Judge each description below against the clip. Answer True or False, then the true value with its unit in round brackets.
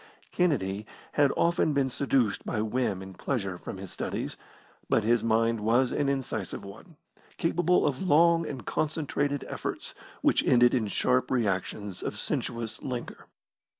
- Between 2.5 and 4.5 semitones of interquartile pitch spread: False (5.0 semitones)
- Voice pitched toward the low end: True (125 Hz)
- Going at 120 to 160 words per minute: True (145 wpm)